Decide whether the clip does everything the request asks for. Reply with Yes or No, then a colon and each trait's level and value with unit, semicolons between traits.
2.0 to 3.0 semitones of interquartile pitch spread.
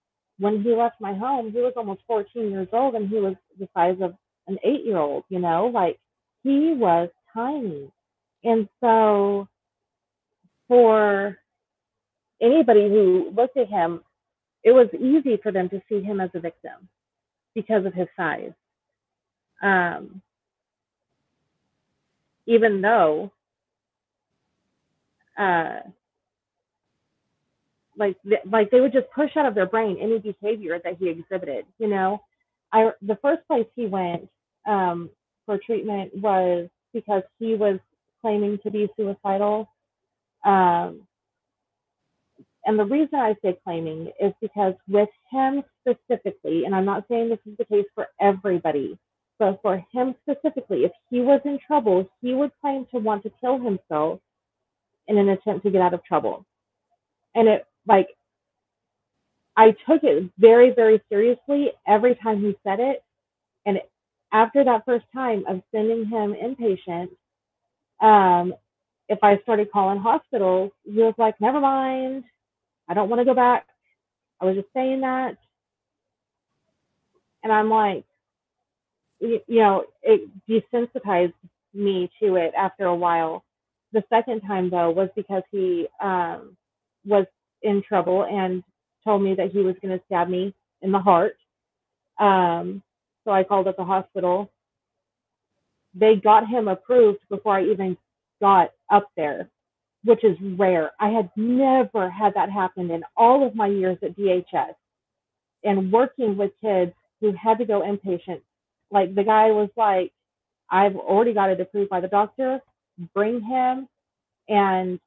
No: average, 3.4 semitones